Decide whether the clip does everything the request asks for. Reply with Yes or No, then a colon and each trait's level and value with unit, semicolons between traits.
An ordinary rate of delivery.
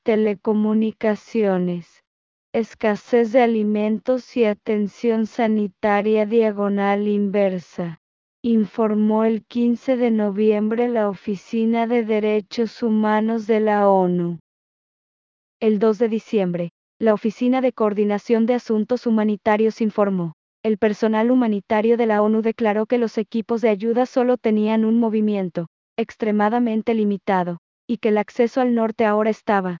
No: slow, 120 wpm